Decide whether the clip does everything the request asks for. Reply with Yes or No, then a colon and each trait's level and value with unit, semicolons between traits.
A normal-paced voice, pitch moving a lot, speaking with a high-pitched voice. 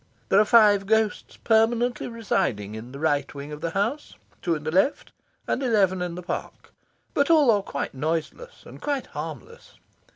Yes: average, 175 wpm; wide, 7.0 semitones; high, 200 Hz